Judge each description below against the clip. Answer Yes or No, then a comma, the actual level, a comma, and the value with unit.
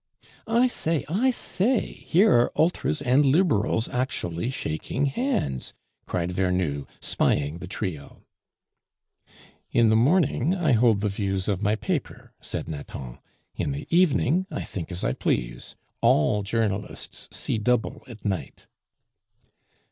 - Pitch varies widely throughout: Yes, wide, 8.6 semitones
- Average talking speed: No, slow, 130 wpm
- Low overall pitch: Yes, low, 115 Hz